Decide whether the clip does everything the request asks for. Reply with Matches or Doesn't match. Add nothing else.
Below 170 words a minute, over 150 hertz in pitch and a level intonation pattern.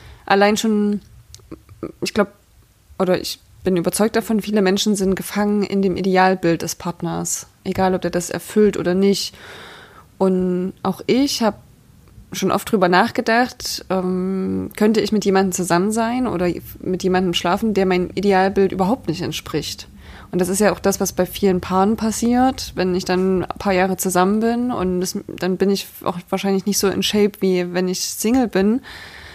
Doesn't match